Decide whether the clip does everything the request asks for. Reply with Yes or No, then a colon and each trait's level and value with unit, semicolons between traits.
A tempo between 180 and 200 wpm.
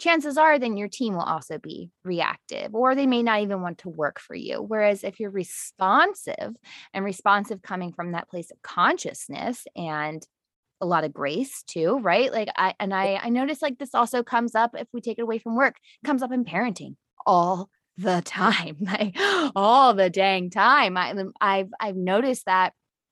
Yes: average, 190 wpm